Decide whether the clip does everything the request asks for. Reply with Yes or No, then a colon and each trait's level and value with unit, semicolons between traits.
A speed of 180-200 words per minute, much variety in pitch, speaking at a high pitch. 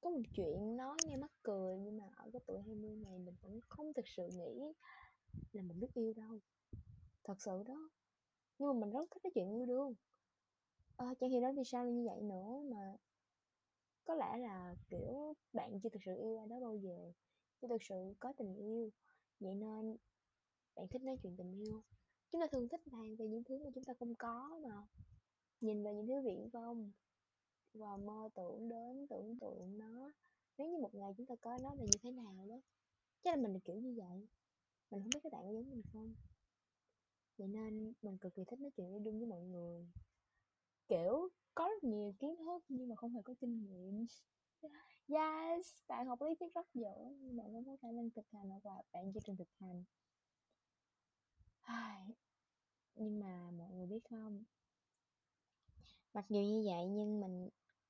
No: average, 195 wpm; average, 4.2 semitones; high, 225 Hz